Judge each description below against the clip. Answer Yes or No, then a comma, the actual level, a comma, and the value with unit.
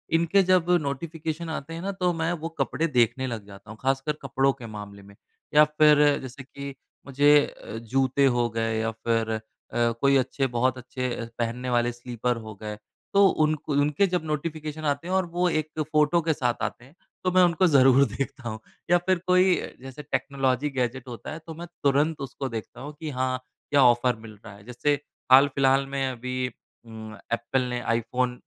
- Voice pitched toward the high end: No, low, 135 Hz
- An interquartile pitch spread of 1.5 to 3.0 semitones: No, average, 4.1 semitones